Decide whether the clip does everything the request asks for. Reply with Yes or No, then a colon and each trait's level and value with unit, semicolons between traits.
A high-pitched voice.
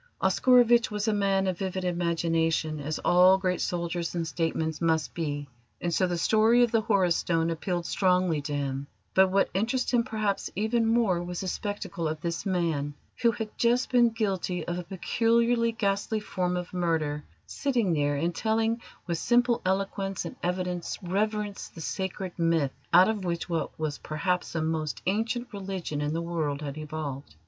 No: medium, 180 Hz